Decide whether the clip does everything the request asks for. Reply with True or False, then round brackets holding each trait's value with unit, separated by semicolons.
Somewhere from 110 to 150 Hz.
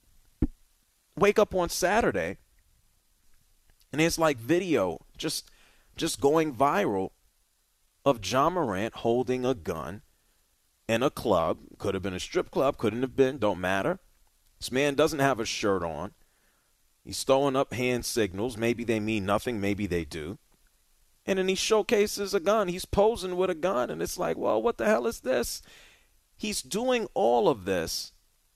True (135 Hz)